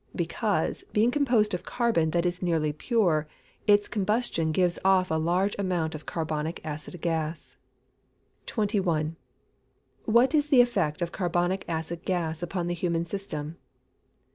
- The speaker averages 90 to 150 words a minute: Yes, average, 140 wpm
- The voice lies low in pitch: No, medium, 175 Hz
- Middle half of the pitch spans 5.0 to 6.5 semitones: No, average, 4.2 semitones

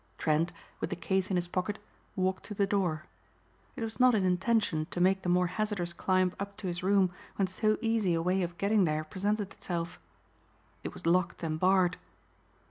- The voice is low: No, medium, 185 Hz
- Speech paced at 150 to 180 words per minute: No, average, 195 wpm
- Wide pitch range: No, narrow, 2.5 semitones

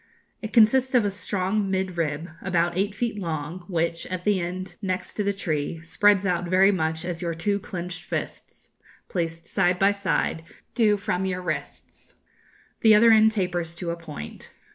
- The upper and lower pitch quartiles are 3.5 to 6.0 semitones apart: No, average, 3.1 semitones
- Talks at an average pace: Yes, average, 175 wpm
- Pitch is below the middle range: No, medium, 185 Hz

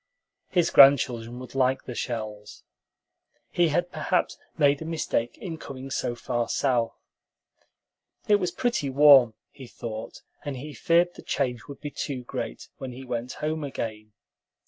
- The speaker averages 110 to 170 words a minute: Yes, average, 150 wpm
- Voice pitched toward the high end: No, low, 135 Hz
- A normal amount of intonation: Yes, average, 4.1 semitones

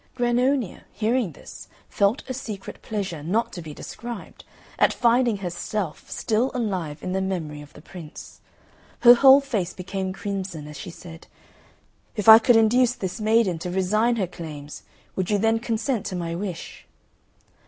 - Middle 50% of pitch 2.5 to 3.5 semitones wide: No, average, 4.8 semitones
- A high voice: Yes, high, 200 Hz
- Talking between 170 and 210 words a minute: No, average, 160 wpm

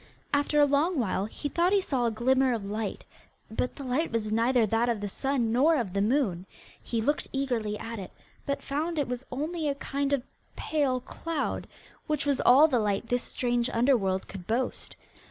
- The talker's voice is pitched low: No, very high, 250 Hz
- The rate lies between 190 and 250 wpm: Yes, average, 195 wpm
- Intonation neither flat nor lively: Yes, average, 4.1 semitones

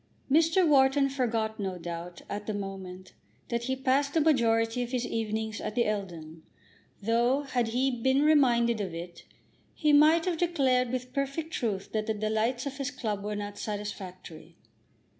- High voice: Yes, high, 235 Hz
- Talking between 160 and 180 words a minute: Yes, average, 165 wpm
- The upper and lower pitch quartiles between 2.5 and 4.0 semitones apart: No, average, 4.6 semitones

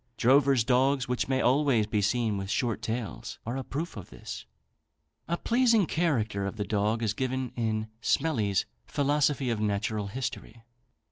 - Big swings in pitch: No, average, 4.1 semitones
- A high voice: No, low, 120 Hz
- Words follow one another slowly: No, average, 155 wpm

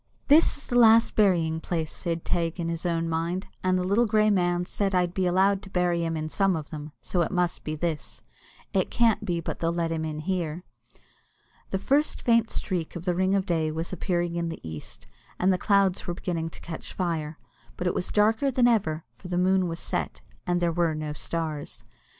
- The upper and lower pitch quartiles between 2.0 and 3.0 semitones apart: Yes, average, 2.7 semitones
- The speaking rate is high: Yes, fast, 215 wpm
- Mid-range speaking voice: Yes, medium, 175 Hz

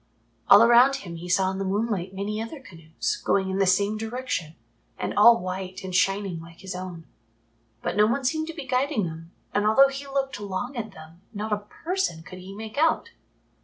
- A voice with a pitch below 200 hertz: No, high, 205 Hz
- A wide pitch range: No, average, 5.0 semitones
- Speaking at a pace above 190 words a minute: Yes, average, 200 wpm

